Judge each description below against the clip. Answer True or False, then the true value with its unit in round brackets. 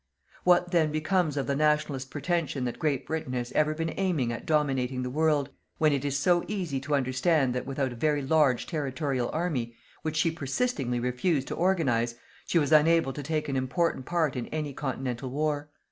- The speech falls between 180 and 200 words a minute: True (190 wpm)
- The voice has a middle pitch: True (145 Hz)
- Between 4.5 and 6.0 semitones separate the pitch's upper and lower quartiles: False (3.4 semitones)